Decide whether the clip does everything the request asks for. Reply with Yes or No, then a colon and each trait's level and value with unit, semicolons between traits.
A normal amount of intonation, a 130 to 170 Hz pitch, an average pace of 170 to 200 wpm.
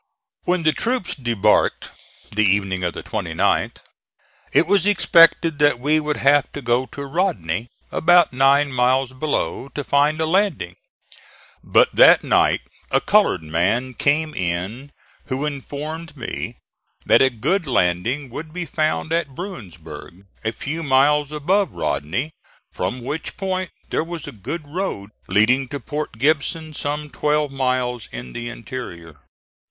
No: average, 4.9 semitones; medium, 140 Hz; average, 145 wpm